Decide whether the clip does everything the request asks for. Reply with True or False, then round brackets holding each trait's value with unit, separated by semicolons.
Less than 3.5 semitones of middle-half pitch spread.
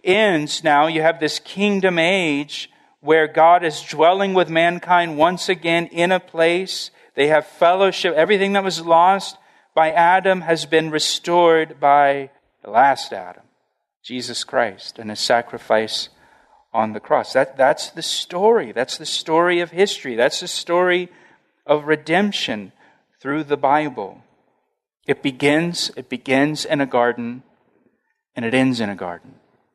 False (3.8 semitones)